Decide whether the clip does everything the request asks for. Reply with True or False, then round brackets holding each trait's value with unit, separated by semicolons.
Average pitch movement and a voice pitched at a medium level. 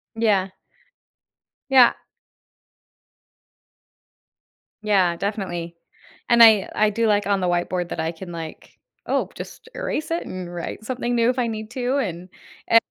False (5.0 semitones; 210 Hz)